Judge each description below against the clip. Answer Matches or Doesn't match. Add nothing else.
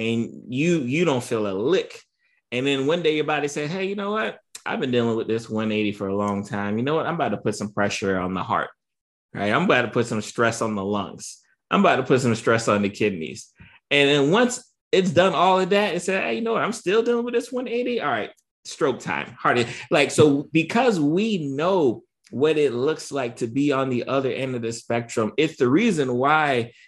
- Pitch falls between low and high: Matches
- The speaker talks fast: Matches